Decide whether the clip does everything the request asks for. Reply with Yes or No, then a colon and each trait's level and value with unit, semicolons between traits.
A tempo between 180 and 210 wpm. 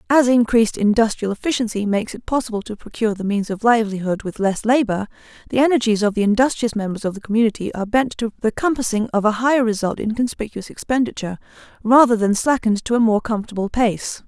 Yes: average, 190 wpm